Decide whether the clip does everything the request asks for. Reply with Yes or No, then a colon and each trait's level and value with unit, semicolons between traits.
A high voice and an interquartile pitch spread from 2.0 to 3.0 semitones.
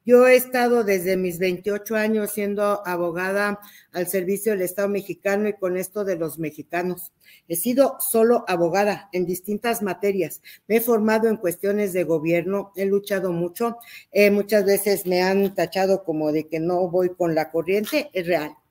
Yes: high, 195 Hz; average, 2.7 semitones